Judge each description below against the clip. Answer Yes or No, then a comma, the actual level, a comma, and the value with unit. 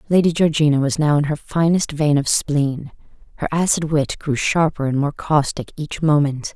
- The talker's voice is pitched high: No, medium, 150 Hz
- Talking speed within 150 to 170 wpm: No, average, 185 wpm